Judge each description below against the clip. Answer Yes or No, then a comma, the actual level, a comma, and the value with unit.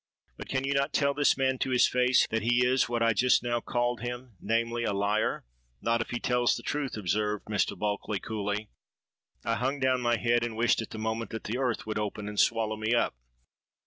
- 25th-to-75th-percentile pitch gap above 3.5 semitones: No, narrow, 2.5 semitones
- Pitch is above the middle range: No, low, 115 Hz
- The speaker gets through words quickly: Yes, fast, 210 wpm